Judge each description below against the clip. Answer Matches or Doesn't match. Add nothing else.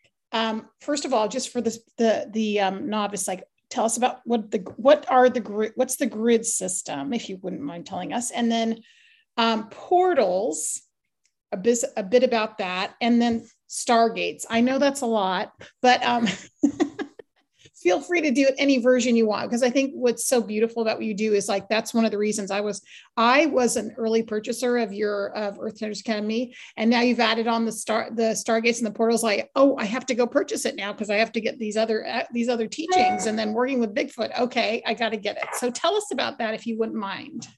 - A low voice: Doesn't match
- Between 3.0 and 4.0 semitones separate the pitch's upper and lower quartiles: Doesn't match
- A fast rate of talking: Matches